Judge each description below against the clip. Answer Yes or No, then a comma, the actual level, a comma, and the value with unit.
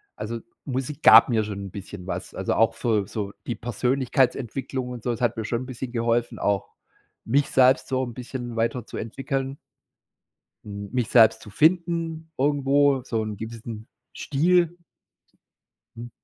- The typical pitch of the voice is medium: No, low, 120 Hz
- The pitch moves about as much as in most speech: Yes, average, 3.3 semitones